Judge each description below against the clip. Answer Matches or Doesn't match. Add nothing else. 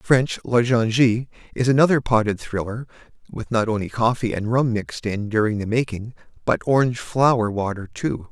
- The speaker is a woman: Doesn't match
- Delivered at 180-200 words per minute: Doesn't match